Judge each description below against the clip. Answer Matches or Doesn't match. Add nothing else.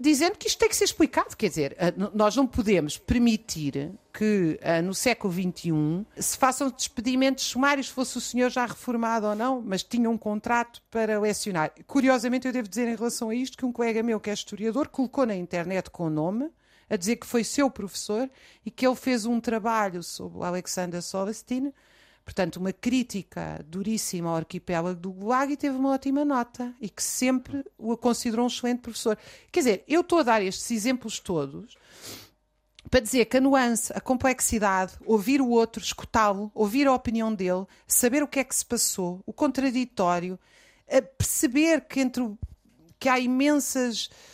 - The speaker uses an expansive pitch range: Doesn't match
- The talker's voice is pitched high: Matches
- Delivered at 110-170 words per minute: Doesn't match